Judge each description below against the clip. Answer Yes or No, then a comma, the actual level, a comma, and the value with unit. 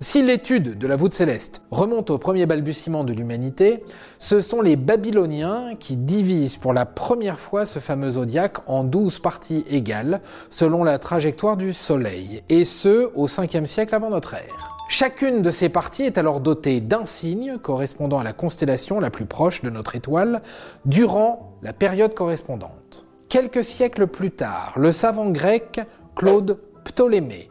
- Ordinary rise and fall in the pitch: No, wide, 7.3 semitones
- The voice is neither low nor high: Yes, medium, 175 Hz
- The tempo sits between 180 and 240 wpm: No, average, 160 wpm